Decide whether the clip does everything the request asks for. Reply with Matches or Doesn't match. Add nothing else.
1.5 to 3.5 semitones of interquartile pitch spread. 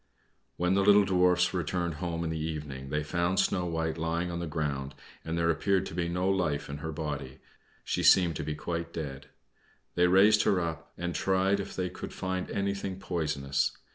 Matches